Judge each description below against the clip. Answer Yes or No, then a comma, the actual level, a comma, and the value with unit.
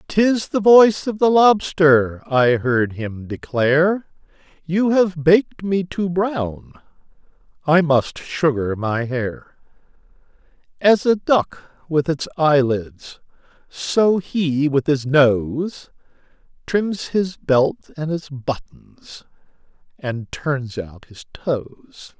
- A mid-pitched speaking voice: Yes, medium, 155 Hz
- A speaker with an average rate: No, slow, 115 wpm